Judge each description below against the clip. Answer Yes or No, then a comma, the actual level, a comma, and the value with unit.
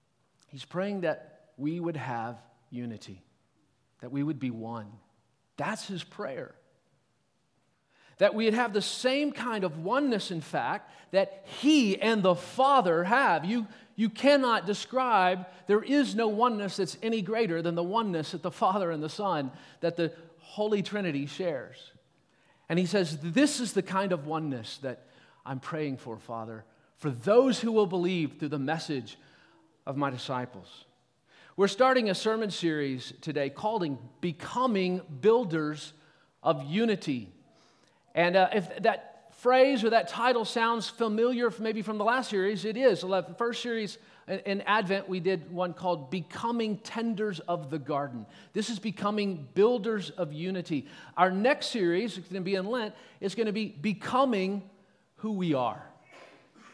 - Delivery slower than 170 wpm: Yes, average, 155 wpm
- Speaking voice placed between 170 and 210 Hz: Yes, medium, 185 Hz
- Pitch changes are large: Yes, wide, 6.1 semitones